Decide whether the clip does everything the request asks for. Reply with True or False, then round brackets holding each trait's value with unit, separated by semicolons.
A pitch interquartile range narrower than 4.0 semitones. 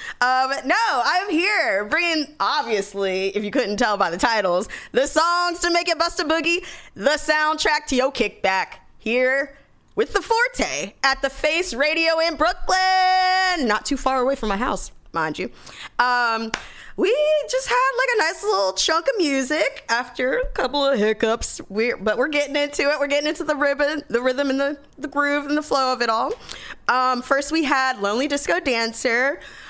False (4.5 semitones)